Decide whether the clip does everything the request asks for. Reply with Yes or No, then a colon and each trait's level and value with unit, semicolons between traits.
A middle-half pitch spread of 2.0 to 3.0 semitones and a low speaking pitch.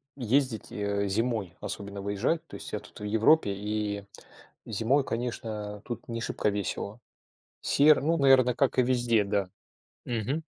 No: average, 3.9 semitones; low, 110 Hz